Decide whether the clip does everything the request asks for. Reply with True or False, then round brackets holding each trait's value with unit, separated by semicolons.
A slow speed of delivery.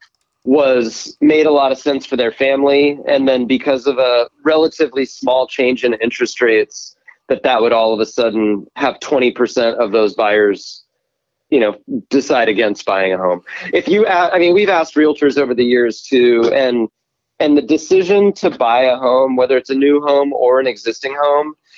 False (185 wpm)